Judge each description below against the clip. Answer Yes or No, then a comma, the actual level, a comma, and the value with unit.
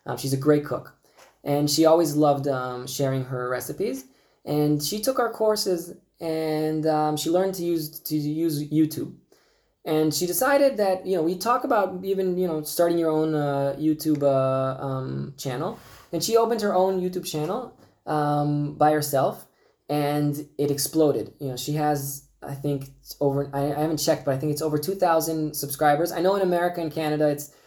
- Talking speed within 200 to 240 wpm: No, average, 190 wpm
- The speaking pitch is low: No, medium, 150 Hz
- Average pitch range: Yes, average, 3.1 semitones